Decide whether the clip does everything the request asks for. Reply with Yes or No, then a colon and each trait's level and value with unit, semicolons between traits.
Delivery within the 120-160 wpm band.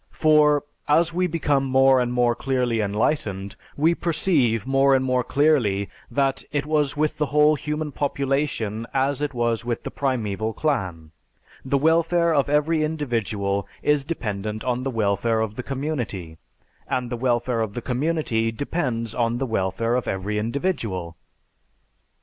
Yes: average, 150 wpm